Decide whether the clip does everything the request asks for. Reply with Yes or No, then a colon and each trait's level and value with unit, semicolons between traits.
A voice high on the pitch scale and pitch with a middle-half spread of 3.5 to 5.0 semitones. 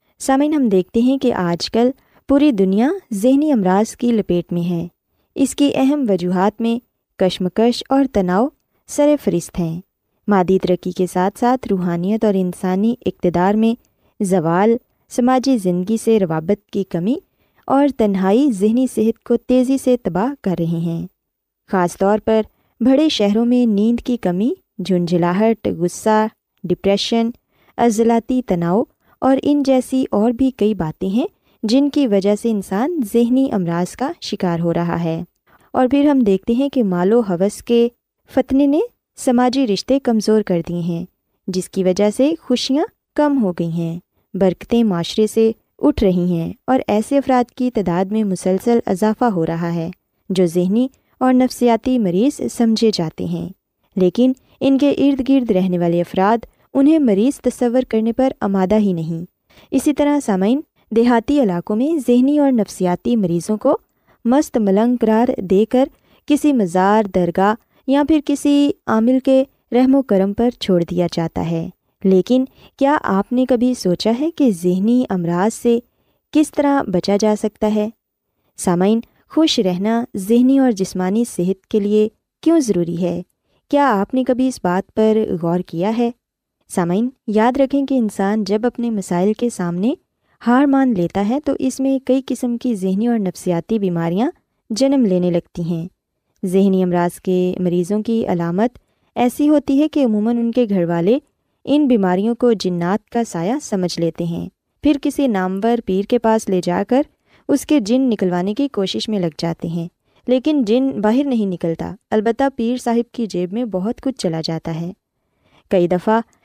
No: high, 220 Hz; wide, 5.5 semitones